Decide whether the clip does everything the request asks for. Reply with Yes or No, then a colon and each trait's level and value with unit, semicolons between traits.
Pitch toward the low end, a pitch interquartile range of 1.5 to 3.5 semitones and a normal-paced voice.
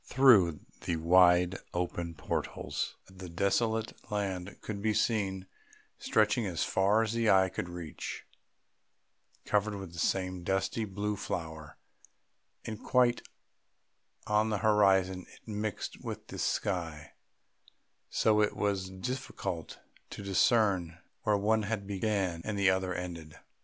No: very low, 95 Hz; average, 3.0 semitones; slow, 130 wpm